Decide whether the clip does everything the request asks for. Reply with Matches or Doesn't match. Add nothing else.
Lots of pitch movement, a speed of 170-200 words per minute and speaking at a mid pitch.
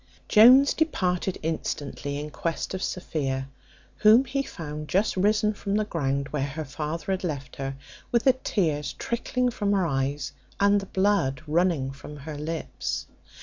Doesn't match